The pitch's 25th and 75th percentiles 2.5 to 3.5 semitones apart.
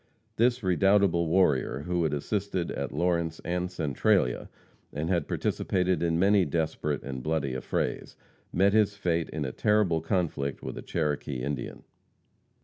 No: average, 4.1 semitones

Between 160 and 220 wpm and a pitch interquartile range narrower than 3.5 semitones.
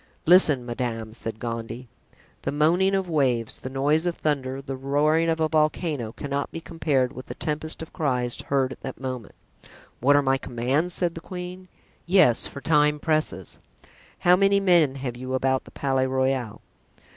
No: average, 170 wpm; average, 3.9 semitones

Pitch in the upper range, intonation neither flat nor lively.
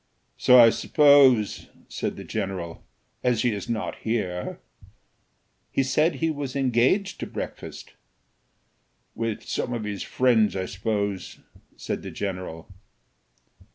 No: low, 115 Hz; average, 4.7 semitones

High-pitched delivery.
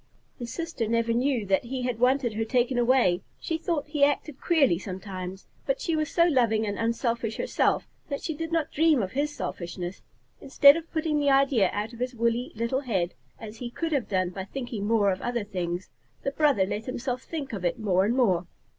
Yes: high, 240 Hz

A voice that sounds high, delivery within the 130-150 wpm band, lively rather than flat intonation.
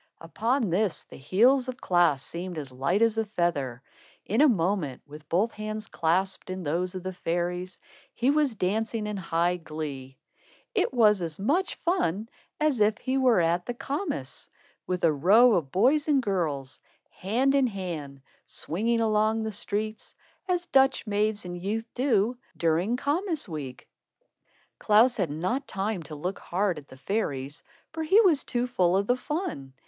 No: high, 200 Hz; average, 165 wpm; wide, 6.2 semitones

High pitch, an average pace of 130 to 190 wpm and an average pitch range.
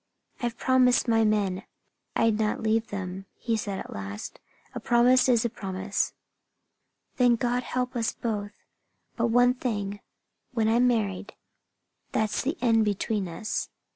Yes: high, 225 Hz; average, 140 wpm; average, 3.0 semitones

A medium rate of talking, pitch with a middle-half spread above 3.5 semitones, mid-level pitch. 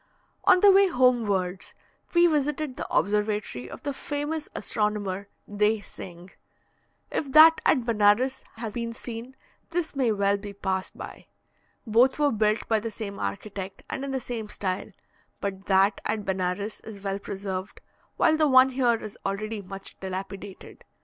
No: average, 155 wpm; average, 4.8 semitones; high, 215 Hz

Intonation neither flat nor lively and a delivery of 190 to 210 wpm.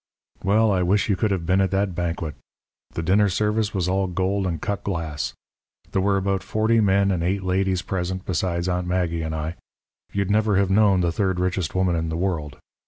No: narrow, 2.2 semitones; fast, 205 wpm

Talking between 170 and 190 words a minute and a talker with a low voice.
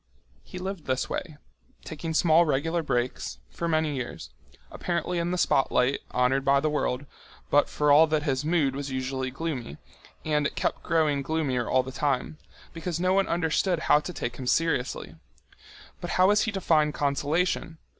No: average, 175 wpm; medium, 150 Hz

